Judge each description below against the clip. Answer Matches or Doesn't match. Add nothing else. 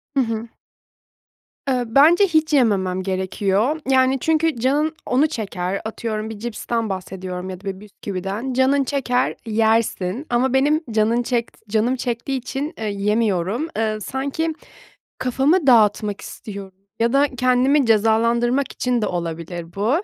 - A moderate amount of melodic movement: Matches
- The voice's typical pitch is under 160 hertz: Doesn't match